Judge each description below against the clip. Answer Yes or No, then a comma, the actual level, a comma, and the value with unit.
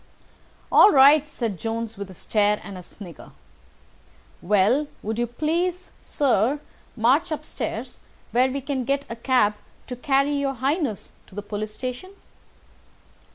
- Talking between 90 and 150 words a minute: Yes, average, 145 wpm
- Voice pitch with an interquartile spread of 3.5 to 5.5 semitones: Yes, average, 4.9 semitones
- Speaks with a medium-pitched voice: No, very high, 250 Hz